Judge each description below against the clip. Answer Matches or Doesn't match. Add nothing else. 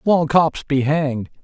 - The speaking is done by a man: Matches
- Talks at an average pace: Matches